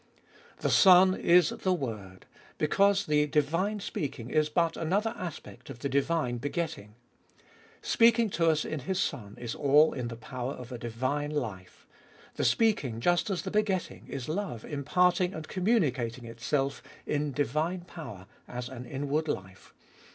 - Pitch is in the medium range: Yes, medium, 150 Hz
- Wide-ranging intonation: Yes, wide, 6.2 semitones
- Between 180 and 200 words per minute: No, average, 155 wpm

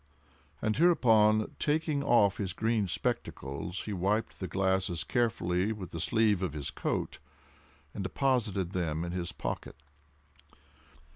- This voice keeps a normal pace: No, slow, 130 wpm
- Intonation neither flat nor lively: Yes, average, 3.8 semitones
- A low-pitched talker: Yes, low, 100 Hz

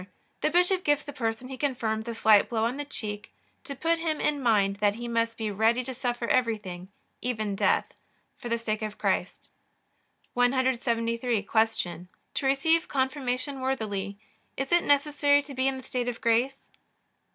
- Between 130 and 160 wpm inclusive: No, average, 170 wpm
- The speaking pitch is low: No, high, 245 Hz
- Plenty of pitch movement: No, average, 3.7 semitones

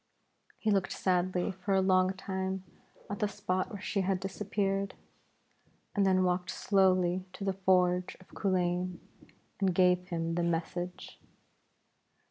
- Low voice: No, medium, 185 Hz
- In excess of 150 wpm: No, slow, 135 wpm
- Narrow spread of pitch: Yes, narrow, 1.3 semitones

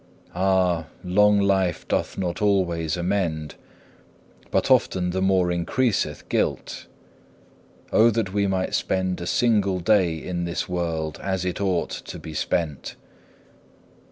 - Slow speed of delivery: Yes, slow, 130 wpm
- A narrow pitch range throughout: Yes, narrow, 2.2 semitones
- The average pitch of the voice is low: Yes, very low, 90 Hz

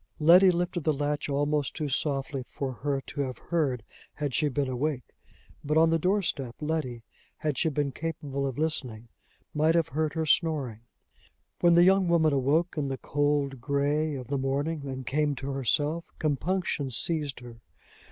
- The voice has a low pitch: No, medium, 145 Hz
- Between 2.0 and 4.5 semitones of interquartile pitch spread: Yes, average, 2.8 semitones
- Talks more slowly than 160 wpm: No, average, 170 wpm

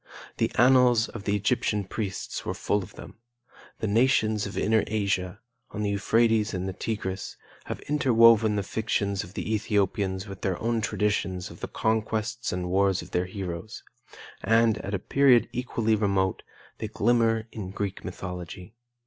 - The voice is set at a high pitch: No, low, 105 Hz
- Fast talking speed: No, average, 155 wpm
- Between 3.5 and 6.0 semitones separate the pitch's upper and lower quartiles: No, average, 2.8 semitones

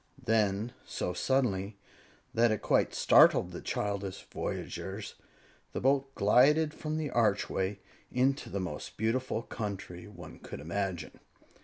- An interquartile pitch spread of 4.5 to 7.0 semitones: Yes, average, 4.9 semitones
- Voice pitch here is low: Yes, low, 105 Hz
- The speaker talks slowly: Yes, slow, 125 wpm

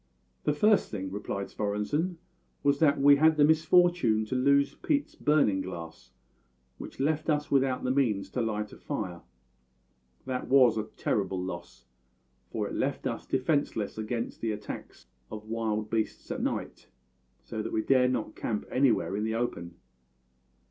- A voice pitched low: Yes, low, 120 Hz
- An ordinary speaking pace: Yes, average, 155 wpm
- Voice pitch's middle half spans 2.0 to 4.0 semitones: No, average, 5.2 semitones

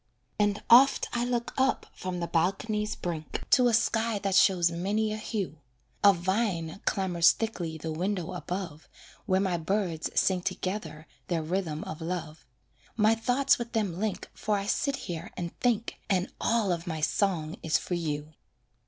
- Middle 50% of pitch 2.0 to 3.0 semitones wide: No, average, 4.2 semitones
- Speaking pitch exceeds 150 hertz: Yes, high, 190 Hz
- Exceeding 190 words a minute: No, average, 165 wpm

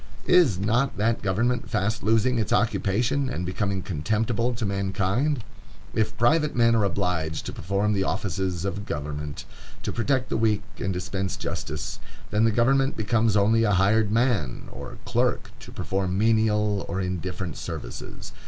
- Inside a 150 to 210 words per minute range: Yes, average, 155 wpm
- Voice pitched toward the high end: No, low, 105 Hz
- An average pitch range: Yes, average, 3.5 semitones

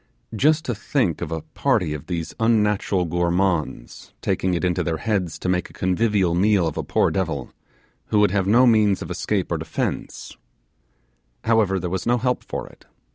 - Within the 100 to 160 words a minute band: No, average, 185 wpm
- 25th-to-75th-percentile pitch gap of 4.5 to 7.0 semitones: No, average, 3.9 semitones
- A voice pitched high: No, very low, 95 Hz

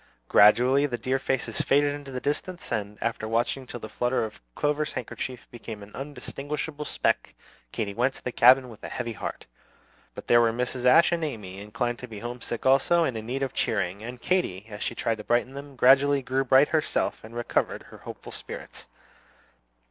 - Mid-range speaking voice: No, low, 125 Hz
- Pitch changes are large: No, average, 3.4 semitones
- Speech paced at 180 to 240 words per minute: Yes, average, 190 wpm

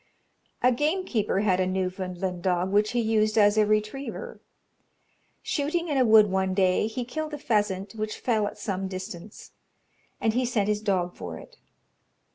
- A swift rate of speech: No, average, 165 wpm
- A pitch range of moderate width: Yes, average, 3.7 semitones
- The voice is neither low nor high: No, high, 210 Hz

